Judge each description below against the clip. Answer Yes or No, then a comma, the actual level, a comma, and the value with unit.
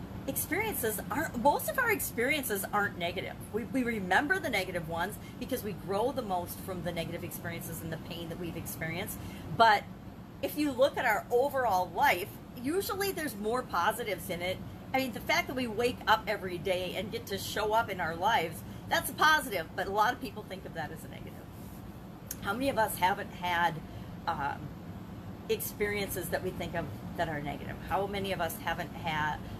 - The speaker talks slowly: No, average, 195 wpm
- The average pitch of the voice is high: Yes, high, 205 Hz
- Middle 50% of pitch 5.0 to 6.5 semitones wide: Yes, wide, 5.6 semitones